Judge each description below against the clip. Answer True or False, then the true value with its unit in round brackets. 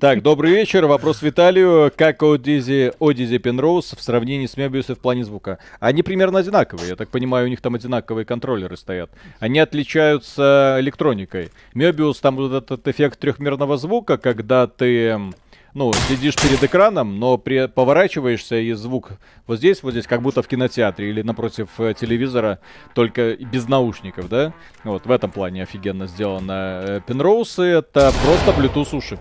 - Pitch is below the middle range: True (125 Hz)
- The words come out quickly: False (150 wpm)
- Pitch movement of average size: True (4.2 semitones)